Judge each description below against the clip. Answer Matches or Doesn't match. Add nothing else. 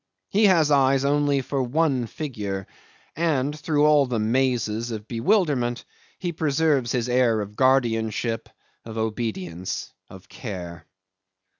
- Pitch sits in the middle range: Doesn't match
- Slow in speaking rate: Matches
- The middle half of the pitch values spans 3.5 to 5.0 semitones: Matches